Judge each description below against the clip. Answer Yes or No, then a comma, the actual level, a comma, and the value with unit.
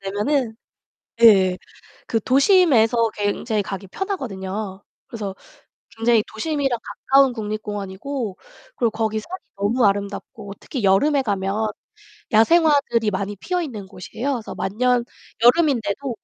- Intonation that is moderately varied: Yes, average, 4.9 semitones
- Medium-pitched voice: No, high, 225 Hz